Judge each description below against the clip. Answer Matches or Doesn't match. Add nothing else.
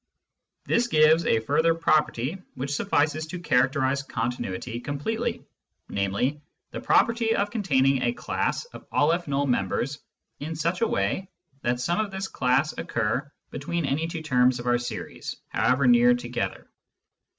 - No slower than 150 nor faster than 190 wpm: Doesn't match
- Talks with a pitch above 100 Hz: Matches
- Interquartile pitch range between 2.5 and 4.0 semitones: Doesn't match